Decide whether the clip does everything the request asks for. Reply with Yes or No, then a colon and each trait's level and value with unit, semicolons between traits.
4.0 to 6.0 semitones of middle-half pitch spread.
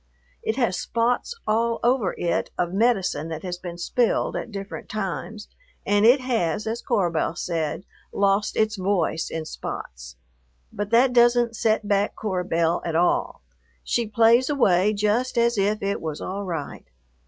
Yes: average, 4.7 semitones